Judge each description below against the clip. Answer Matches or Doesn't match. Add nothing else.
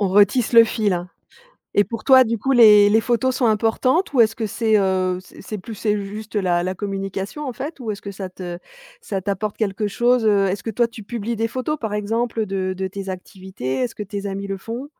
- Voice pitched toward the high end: Matches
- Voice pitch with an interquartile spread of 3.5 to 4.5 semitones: Doesn't match